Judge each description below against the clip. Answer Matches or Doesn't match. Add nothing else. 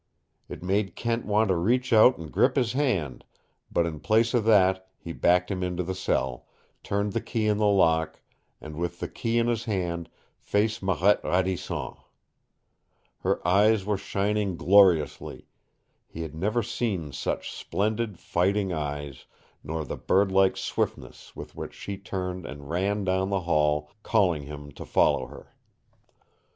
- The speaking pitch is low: Matches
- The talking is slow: Doesn't match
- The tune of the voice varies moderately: Matches